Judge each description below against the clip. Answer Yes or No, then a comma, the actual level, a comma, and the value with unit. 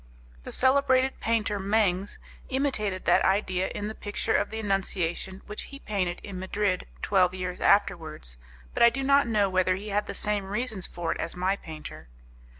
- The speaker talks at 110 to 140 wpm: No, average, 175 wpm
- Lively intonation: No, average, 3.1 semitones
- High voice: Yes, high, 200 Hz